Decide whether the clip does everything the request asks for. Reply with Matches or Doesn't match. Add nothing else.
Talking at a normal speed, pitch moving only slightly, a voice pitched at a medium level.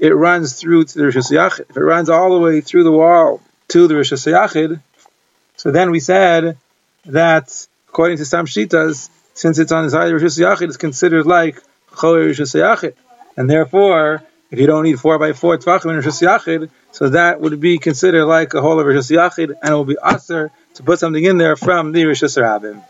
Matches